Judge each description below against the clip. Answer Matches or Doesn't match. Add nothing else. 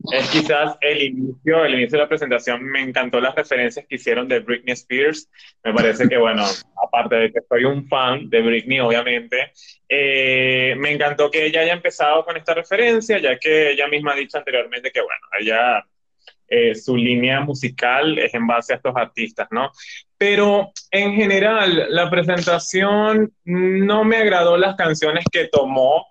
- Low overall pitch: Doesn't match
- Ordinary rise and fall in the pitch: Doesn't match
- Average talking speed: Matches